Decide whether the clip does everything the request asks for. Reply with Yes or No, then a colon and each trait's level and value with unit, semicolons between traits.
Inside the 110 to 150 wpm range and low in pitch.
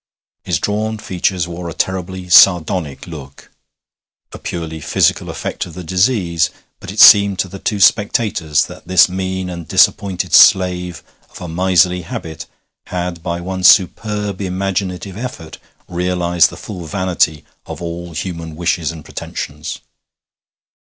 Yes: slow, 135 wpm; very low, 90 Hz